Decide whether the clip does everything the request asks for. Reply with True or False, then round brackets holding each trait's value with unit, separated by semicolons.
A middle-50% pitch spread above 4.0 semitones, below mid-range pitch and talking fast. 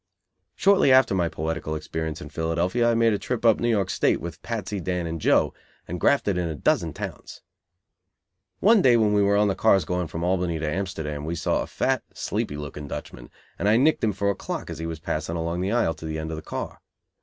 True (4.6 semitones; 90 Hz; 230 wpm)